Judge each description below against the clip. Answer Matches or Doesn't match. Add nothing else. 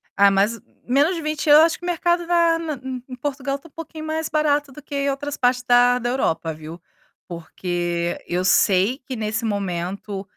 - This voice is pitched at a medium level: Doesn't match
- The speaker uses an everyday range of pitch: Doesn't match